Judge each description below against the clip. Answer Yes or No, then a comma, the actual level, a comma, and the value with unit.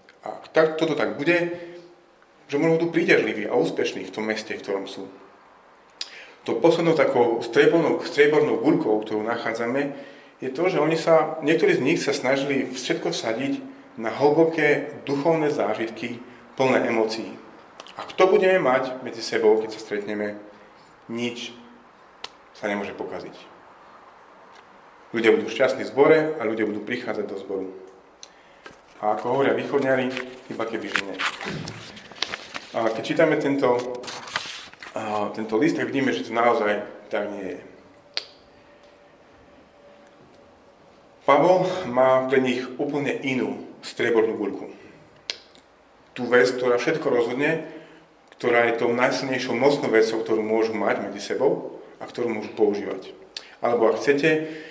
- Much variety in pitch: Yes, wide, 5.8 semitones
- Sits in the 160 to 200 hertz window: No, low, 130 Hz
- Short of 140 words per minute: Yes, average, 130 wpm